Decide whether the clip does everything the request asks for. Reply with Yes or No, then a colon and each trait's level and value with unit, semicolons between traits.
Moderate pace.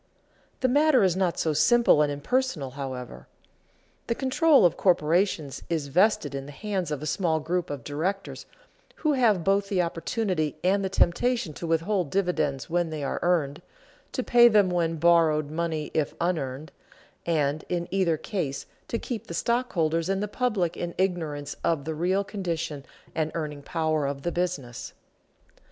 Yes: average, 165 wpm